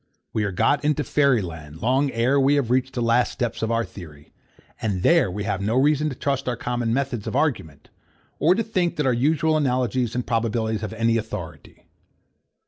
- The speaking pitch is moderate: No, low, 120 Hz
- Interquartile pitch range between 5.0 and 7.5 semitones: No, average, 4.1 semitones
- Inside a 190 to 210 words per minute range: Yes, average, 200 wpm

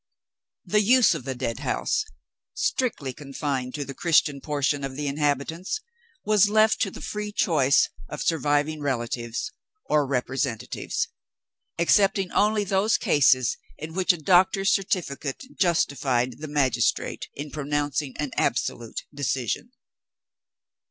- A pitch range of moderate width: No, wide, 5.8 semitones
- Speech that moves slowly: Yes, slow, 120 wpm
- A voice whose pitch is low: No, medium, 145 Hz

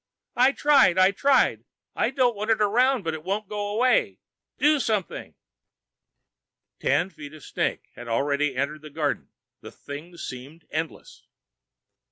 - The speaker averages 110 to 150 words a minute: Yes, average, 145 wpm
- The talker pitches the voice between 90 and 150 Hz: No, medium, 185 Hz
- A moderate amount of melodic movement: No, wide, 7.4 semitones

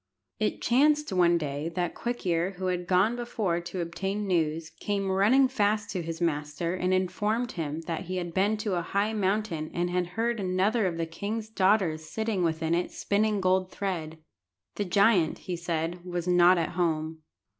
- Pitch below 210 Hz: Yes, medium, 185 Hz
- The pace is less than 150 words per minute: No, average, 180 wpm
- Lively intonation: No, average, 3.5 semitones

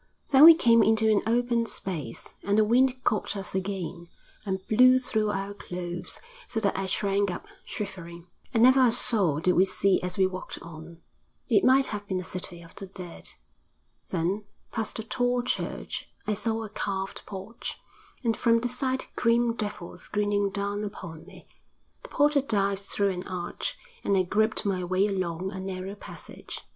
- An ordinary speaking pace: Yes, average, 175 wpm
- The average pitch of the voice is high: Yes, high, 200 Hz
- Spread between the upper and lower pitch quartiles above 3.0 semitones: Yes, average, 3.6 semitones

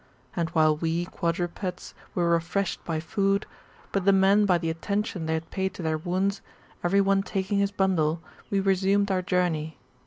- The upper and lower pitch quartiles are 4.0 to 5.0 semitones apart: No, average, 2.9 semitones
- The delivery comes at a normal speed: Yes, average, 175 wpm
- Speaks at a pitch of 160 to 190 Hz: Yes, medium, 185 Hz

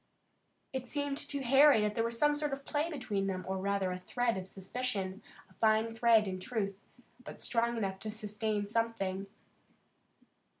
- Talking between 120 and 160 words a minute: No, average, 170 wpm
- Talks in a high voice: Yes, high, 220 Hz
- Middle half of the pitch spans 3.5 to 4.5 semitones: Yes, average, 4.2 semitones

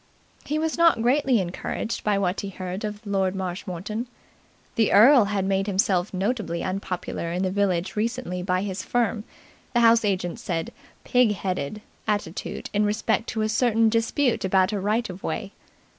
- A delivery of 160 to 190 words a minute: Yes, average, 165 wpm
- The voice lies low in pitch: No, high, 205 Hz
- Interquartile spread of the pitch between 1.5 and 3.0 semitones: No, average, 3.4 semitones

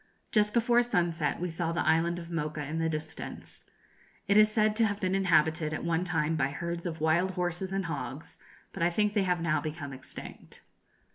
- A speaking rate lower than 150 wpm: No, average, 200 wpm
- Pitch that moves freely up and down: No, average, 3.2 semitones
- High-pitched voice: No, medium, 170 Hz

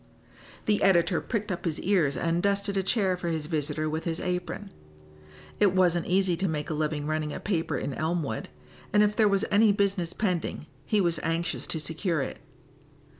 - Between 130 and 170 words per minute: No, average, 185 wpm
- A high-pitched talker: No, medium, 175 Hz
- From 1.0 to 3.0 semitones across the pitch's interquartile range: No, average, 3.7 semitones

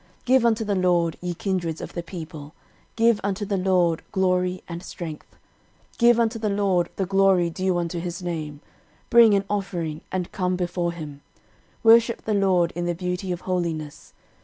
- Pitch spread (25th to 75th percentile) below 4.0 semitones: Yes, narrow, 2.6 semitones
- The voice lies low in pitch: No, medium, 180 Hz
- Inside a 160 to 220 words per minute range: Yes, average, 180 wpm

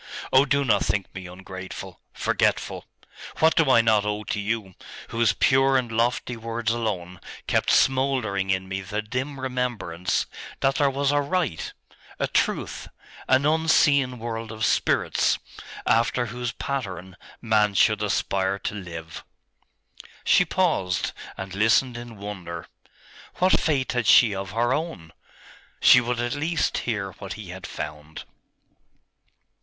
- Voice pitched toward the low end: Yes, low, 115 Hz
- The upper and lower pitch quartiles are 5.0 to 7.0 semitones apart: Yes, wide, 5.4 semitones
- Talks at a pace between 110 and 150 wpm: Yes, average, 140 wpm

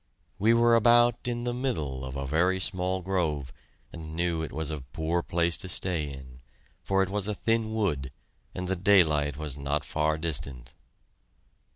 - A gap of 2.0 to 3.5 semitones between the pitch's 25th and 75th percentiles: No, wide, 5.4 semitones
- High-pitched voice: No, very low, 85 Hz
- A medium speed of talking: Yes, average, 175 wpm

